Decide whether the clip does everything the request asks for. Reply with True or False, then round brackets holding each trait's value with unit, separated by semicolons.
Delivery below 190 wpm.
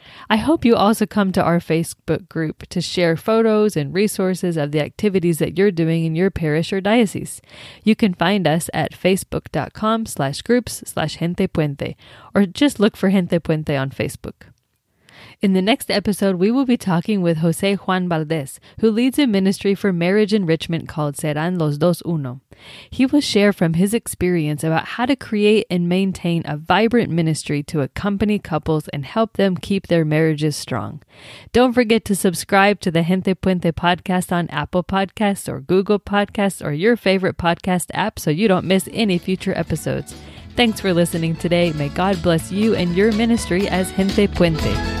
True (180 wpm)